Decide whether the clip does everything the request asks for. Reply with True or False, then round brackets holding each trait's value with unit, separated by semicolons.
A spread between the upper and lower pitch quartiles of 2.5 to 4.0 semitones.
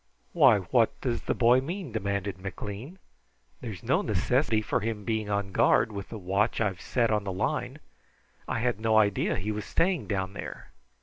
True (2.9 semitones)